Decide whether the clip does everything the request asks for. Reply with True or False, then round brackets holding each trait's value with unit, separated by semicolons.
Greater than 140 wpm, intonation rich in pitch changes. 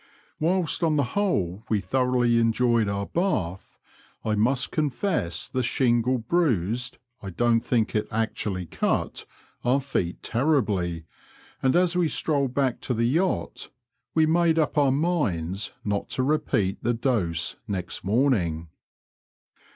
False (135 wpm; 6.2 semitones)